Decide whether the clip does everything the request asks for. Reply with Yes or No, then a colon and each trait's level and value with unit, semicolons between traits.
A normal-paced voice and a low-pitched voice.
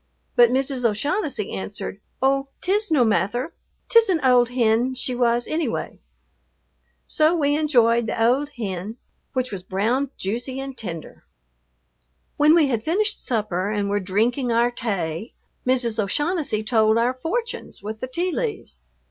No: average, 150 wpm; high, 245 Hz